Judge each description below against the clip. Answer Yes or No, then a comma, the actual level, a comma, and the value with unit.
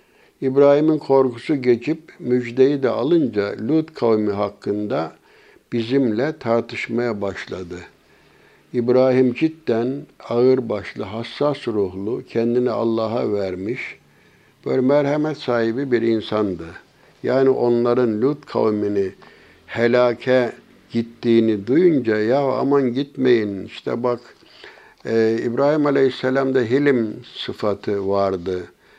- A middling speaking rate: No, slow, 85 wpm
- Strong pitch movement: No, average, 3.4 semitones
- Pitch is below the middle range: Yes, low, 120 Hz